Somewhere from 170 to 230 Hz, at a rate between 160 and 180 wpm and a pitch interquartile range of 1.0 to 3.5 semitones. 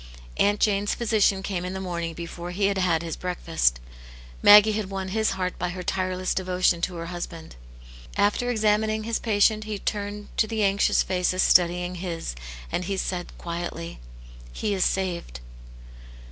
Yes: medium, 185 Hz; average, 170 wpm; average, 2.8 semitones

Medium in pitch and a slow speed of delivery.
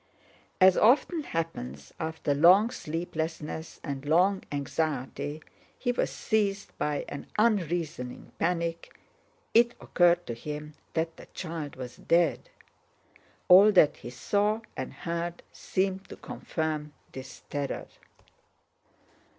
Yes: medium, 165 Hz; slow, 110 wpm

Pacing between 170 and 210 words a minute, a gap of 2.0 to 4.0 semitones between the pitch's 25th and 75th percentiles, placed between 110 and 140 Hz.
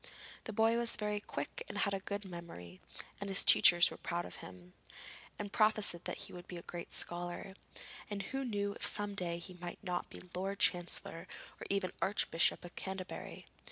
No: average, 190 wpm; average, 2.8 semitones; high, 190 Hz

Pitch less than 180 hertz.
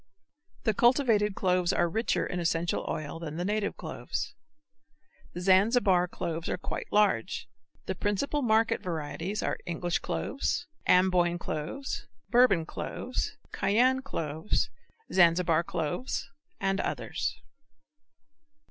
No: medium, 185 Hz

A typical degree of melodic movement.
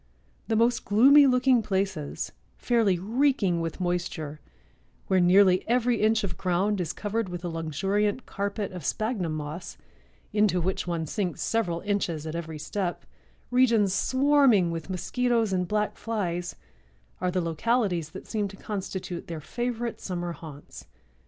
Yes: average, 4.5 semitones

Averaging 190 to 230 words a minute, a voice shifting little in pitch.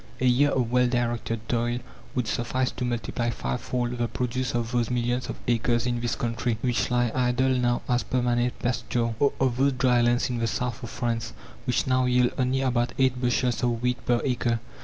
Yes: average, 200 wpm; narrow, 0.9 semitones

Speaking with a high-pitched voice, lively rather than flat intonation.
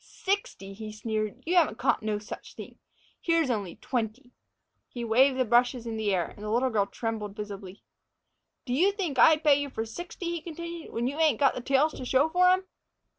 Yes: very high, 250 Hz; wide, 6.5 semitones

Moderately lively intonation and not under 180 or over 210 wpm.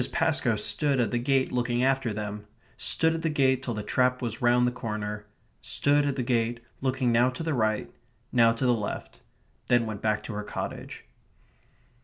Yes: average, 3.1 semitones; average, 190 wpm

